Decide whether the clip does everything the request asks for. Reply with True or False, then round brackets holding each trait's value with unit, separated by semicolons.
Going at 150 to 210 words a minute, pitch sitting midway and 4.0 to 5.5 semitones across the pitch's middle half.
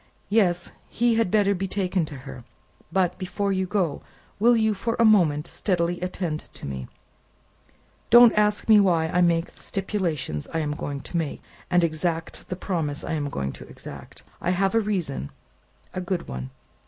True (180 wpm; 180 Hz; 4.3 semitones)